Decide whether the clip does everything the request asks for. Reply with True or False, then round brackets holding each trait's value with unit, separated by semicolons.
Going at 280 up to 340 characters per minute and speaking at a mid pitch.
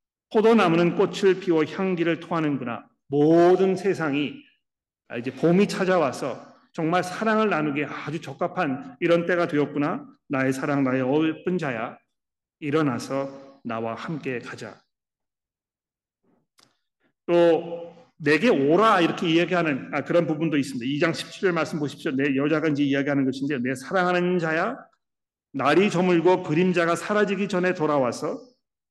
True (295 characters per minute; 165 Hz)